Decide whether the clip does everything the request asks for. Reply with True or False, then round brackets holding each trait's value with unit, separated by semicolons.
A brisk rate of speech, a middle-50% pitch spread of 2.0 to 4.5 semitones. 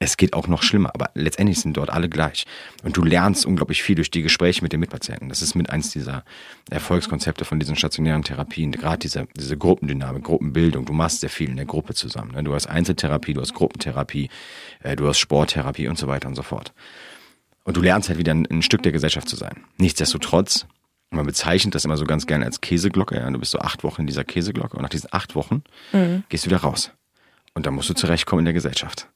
True (220 wpm; 2.8 semitones)